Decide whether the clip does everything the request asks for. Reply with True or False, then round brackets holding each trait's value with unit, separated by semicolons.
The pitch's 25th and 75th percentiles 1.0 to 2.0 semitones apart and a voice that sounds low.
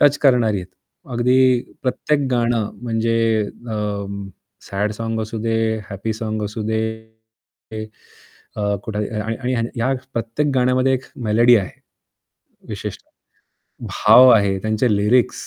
False (2.6 semitones; 115 Hz)